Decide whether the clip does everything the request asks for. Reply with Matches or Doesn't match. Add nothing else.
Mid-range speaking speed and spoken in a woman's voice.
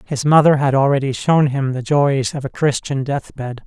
Doesn't match